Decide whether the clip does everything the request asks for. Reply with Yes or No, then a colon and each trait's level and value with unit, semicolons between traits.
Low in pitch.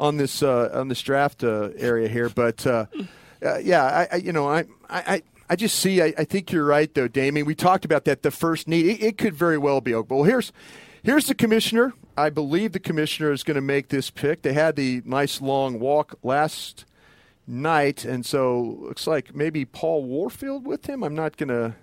No: medium, 150 Hz